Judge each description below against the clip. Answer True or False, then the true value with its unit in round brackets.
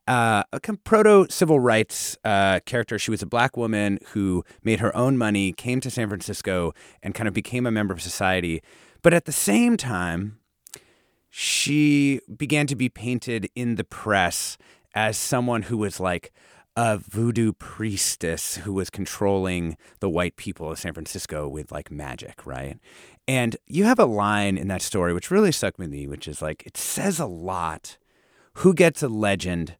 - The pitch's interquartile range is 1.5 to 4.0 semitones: False (5.2 semitones)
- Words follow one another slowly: False (180 wpm)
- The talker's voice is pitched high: False (105 Hz)